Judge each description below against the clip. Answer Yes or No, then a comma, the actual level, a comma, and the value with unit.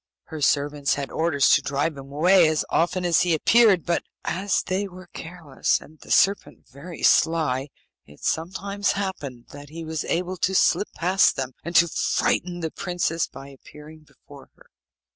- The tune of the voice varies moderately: Yes, average, 3.9 semitones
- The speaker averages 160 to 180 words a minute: Yes, average, 170 wpm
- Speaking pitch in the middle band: Yes, medium, 165 Hz